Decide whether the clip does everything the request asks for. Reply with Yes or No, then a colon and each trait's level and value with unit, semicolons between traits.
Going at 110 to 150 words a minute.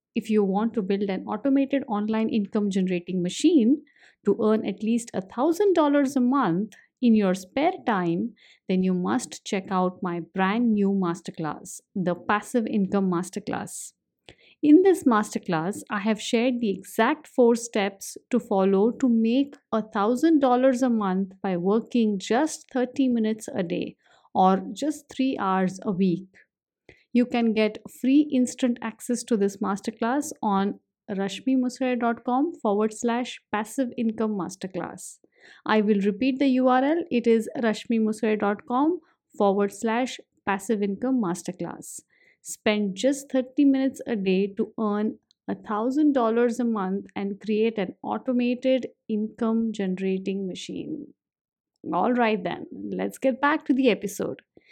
Yes: slow, 135 wpm